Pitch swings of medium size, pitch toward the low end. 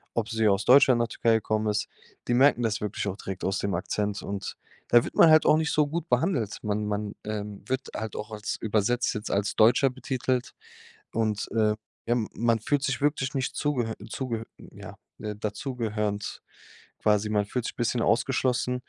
Yes: average, 3.3 semitones; low, 110 Hz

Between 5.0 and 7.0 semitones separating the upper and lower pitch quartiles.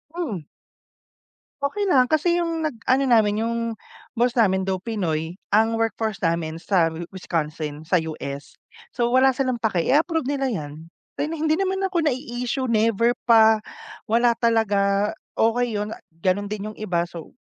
Yes: wide, 5.4 semitones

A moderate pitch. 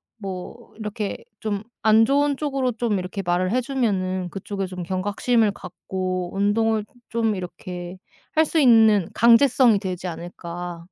No: high, 205 Hz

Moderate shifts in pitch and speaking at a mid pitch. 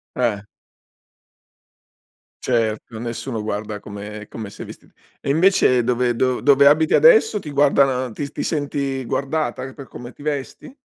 No: average, 3.9 semitones; low, 130 Hz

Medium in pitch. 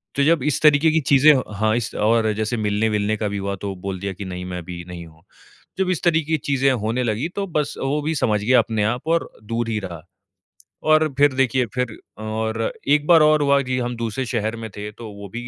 No: low, 115 Hz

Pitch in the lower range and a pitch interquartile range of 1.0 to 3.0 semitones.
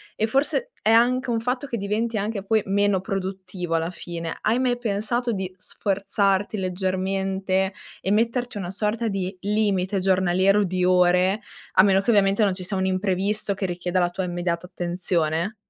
No: high, 195 Hz; narrow, 2.6 semitones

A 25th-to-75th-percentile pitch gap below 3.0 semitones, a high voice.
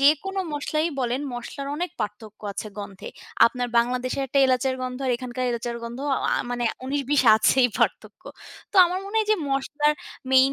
No: average, 3.3 semitones; very high, 260 Hz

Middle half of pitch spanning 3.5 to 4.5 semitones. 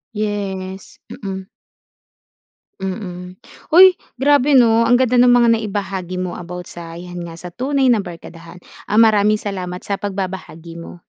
Yes: average, 3.9 semitones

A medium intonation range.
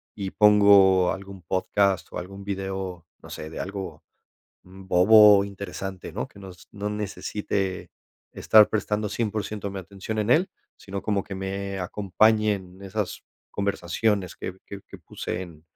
No: narrow, 1.7 semitones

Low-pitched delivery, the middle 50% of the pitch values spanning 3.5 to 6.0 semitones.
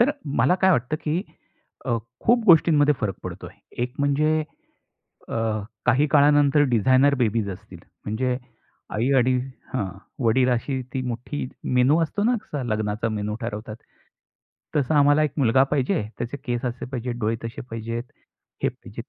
Yes: low, 130 Hz; average, 4.1 semitones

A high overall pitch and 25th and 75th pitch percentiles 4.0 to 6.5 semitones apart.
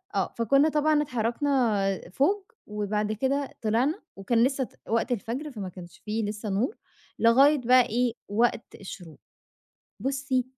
Yes: high, 235 Hz; average, 4.6 semitones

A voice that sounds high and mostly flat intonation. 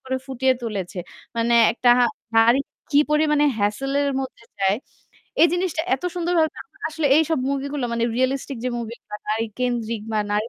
No: very high, 260 Hz; average, 4.3 semitones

